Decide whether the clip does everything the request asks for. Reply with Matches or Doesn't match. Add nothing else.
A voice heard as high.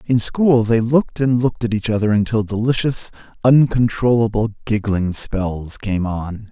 Doesn't match